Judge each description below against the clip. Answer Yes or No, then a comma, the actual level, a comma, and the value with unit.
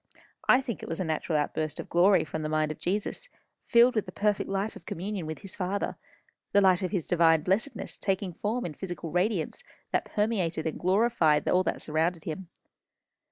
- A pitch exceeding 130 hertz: Yes, medium, 185 Hz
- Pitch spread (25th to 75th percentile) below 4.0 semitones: No, average, 4.3 semitones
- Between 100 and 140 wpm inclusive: No, average, 195 wpm